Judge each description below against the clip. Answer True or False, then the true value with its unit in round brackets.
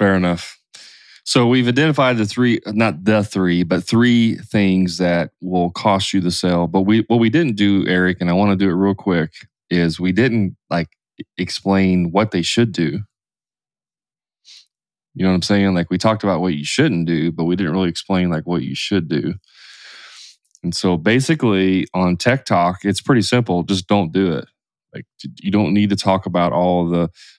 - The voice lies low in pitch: True (95 Hz)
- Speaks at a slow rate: False (195 wpm)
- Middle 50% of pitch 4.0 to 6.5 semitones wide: False (3.3 semitones)